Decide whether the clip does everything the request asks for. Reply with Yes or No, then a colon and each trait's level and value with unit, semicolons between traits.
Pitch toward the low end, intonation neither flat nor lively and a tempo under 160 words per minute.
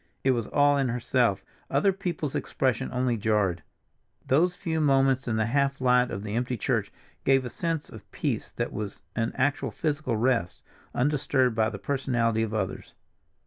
No: low, 130 Hz; average, 3.8 semitones; average, 165 wpm